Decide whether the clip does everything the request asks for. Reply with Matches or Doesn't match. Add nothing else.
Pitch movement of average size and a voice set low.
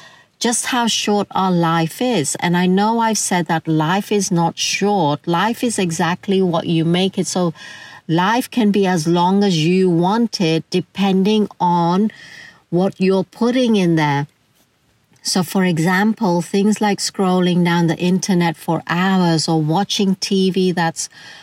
Doesn't match